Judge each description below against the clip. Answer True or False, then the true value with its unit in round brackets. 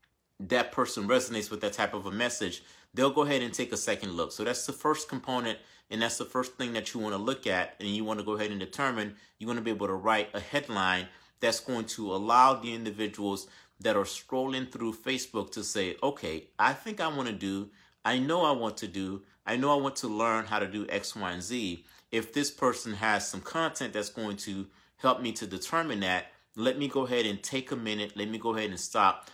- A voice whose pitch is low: True (110 Hz)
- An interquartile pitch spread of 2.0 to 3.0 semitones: False (3.7 semitones)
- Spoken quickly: True (240 wpm)